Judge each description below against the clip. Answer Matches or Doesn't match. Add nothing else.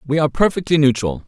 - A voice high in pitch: Doesn't match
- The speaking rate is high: Doesn't match